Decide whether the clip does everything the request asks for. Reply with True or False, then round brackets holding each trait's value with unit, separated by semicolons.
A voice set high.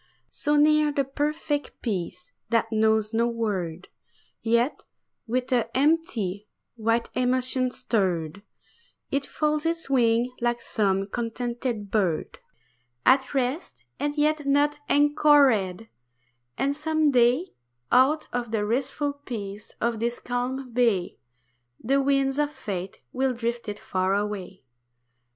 True (245 Hz)